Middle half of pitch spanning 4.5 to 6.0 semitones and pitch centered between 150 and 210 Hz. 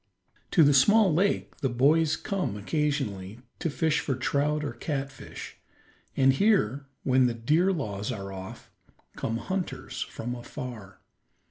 No: average, 5.0 semitones; low, 135 Hz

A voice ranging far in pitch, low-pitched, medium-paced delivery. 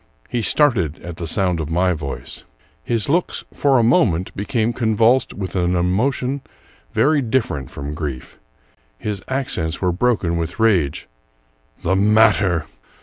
Yes: wide, 6.0 semitones; very low, 95 Hz; average, 145 wpm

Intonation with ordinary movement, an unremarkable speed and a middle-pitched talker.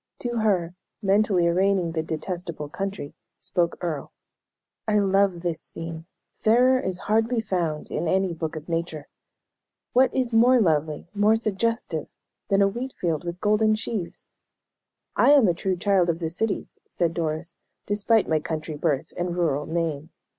Yes: average, 4.5 semitones; average, 155 wpm; medium, 180 Hz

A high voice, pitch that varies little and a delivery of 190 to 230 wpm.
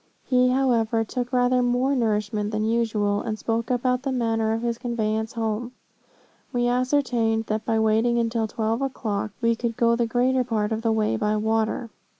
No: high, 230 Hz; narrow, 2.0 semitones; average, 175 wpm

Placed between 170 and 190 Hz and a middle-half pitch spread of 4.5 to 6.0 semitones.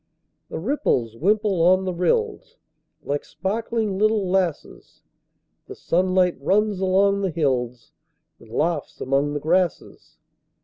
Yes: medium, 185 Hz; average, 5.2 semitones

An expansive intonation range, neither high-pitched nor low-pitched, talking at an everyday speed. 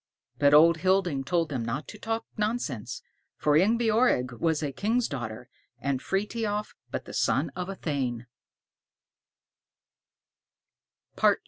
No: wide, 7.6 semitones; medium, 165 Hz; slow, 120 wpm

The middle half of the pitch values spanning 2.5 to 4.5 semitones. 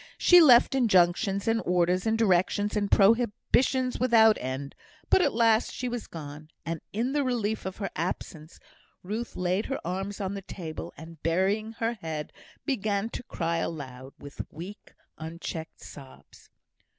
No: wide, 5.4 semitones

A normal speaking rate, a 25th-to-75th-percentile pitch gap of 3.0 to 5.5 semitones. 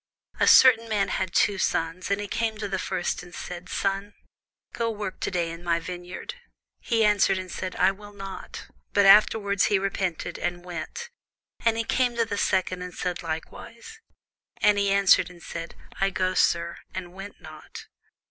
No: average, 180 wpm; narrow, 2.6 semitones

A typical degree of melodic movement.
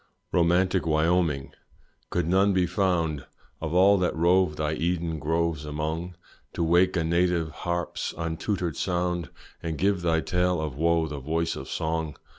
No: narrow, 2.1 semitones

